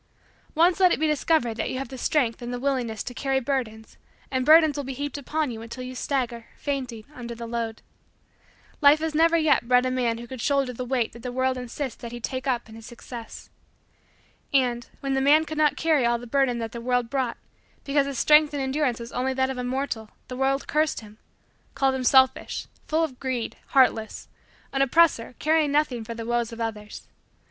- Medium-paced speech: No, fast, 215 wpm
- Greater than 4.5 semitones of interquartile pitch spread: No, average, 3.1 semitones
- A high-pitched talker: Yes, very high, 255 Hz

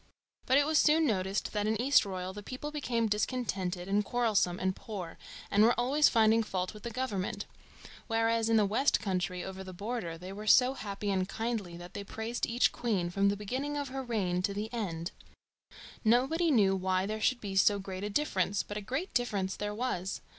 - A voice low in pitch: No, high, 210 Hz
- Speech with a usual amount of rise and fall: Yes, average, 4.1 semitones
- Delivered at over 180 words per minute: Yes, average, 200 wpm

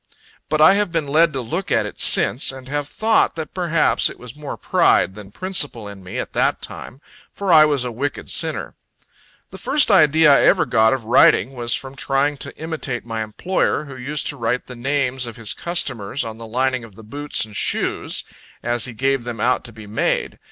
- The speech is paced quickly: Yes, fast, 210 wpm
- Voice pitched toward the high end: No, low, 135 Hz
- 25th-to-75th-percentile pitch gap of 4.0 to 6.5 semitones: Yes, average, 4.4 semitones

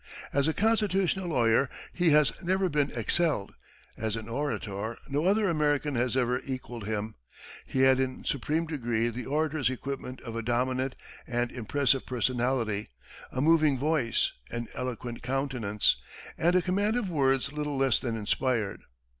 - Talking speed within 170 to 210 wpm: No, average, 150 wpm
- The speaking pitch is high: No, low, 130 Hz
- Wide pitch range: No, average, 4.3 semitones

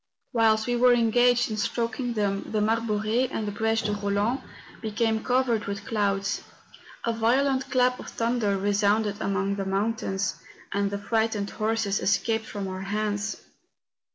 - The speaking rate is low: No, average, 155 wpm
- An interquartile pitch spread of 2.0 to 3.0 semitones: Yes, narrow, 2.4 semitones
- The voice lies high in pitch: Yes, high, 220 Hz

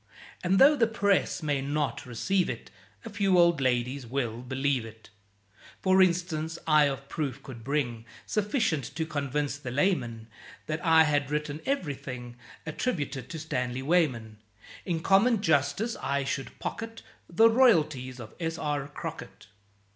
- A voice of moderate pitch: Yes, medium, 150 Hz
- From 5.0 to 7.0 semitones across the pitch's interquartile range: Yes, average, 5.3 semitones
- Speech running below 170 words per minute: Yes, average, 145 wpm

